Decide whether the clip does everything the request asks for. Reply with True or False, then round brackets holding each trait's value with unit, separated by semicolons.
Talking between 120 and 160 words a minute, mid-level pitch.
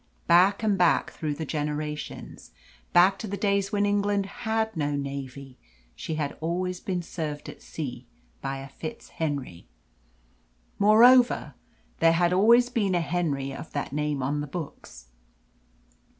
True (140 wpm; 165 Hz)